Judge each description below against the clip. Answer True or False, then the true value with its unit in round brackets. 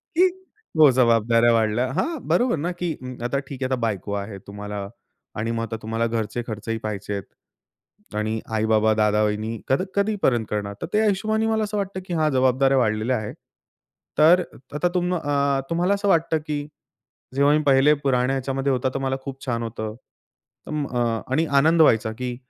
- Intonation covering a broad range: True (6.0 semitones)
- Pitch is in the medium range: False (130 Hz)